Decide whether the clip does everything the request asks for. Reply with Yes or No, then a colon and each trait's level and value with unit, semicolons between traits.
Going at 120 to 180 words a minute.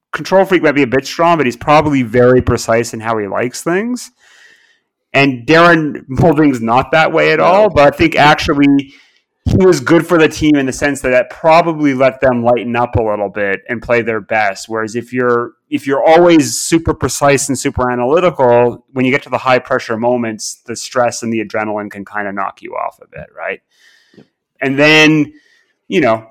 No: fast, 205 wpm